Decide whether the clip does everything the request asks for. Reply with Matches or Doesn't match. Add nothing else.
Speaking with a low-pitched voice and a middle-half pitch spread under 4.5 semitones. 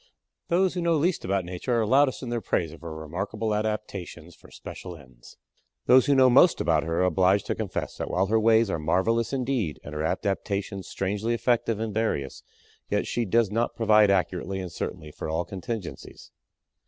Doesn't match